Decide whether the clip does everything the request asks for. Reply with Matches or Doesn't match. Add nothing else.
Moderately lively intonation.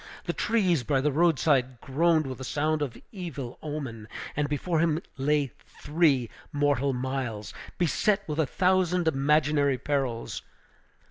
Matches